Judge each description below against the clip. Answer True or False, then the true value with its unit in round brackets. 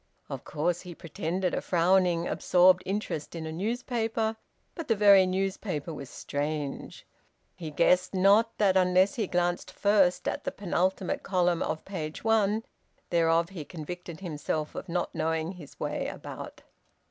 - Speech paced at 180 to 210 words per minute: False (145 wpm)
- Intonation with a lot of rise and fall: False (3.0 semitones)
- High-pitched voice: False (180 Hz)